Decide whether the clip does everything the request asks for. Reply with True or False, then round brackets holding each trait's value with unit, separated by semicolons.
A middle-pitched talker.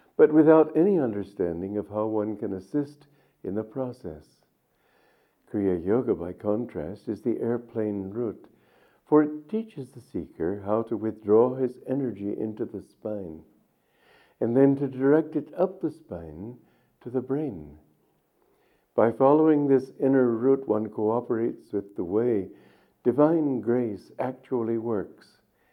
False (120 Hz)